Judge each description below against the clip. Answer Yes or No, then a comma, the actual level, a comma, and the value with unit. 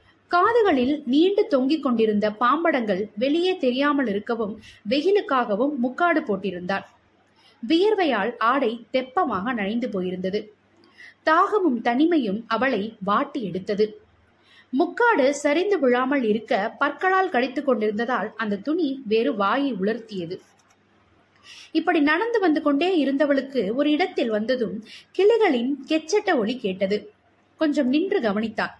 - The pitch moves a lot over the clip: Yes, wide, 6.5 semitones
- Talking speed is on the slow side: No, average, 100 wpm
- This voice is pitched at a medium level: No, very high, 265 Hz